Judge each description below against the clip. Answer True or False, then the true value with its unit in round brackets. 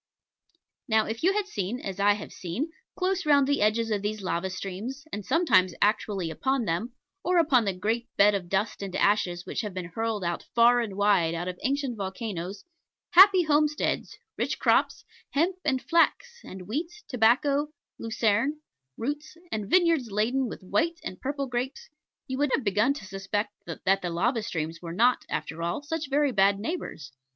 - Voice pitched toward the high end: True (225 Hz)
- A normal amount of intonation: False (6.5 semitones)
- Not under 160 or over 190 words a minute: True (175 wpm)